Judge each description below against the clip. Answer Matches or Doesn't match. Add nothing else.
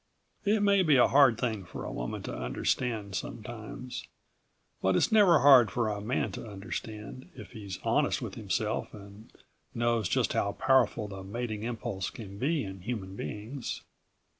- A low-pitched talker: Matches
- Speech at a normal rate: Matches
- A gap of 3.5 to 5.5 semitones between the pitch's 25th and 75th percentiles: Matches